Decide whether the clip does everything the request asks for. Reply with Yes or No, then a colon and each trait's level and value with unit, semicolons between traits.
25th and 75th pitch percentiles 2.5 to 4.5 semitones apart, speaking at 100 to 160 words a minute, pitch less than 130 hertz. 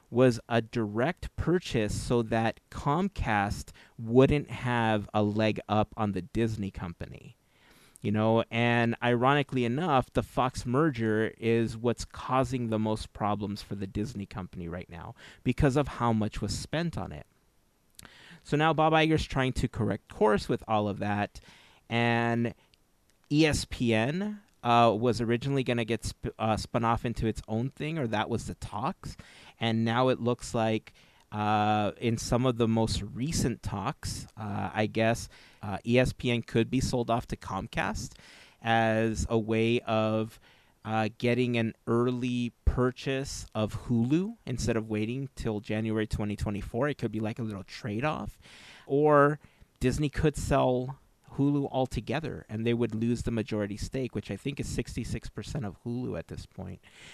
Yes: average, 2.9 semitones; average, 155 wpm; low, 115 Hz